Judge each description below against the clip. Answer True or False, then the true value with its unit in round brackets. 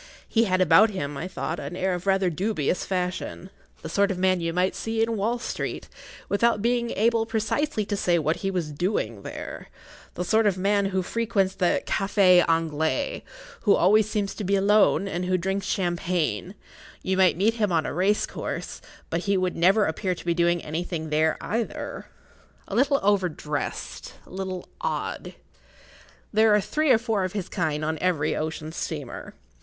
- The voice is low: False (185 Hz)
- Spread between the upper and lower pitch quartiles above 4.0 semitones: False (3.5 semitones)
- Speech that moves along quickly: False (180 wpm)